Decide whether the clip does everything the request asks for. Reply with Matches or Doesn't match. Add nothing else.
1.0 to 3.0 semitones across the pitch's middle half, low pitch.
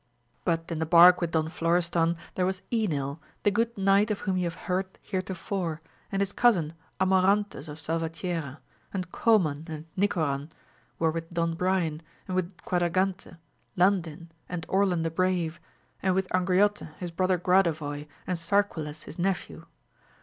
Doesn't match